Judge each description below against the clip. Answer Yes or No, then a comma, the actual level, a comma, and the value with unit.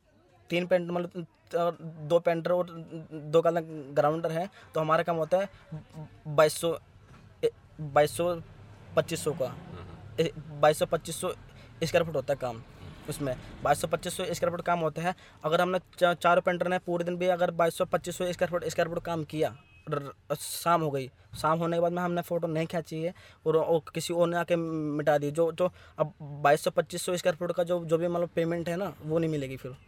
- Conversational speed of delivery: No, fast, 210 wpm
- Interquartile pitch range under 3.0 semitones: Yes, narrow, 2.5 semitones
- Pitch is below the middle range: No, medium, 165 Hz